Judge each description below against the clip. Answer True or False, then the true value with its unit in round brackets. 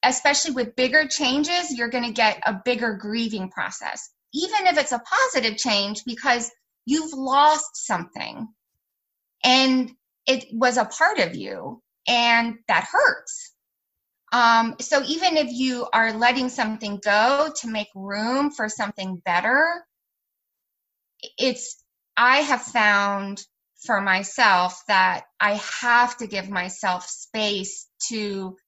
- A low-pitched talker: False (240 Hz)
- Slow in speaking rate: True (130 wpm)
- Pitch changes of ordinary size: True (4.4 semitones)